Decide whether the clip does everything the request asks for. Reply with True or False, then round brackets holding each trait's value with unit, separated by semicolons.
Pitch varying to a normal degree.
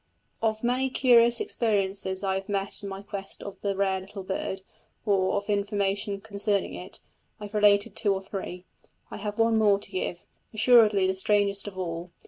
False (1.6 semitones)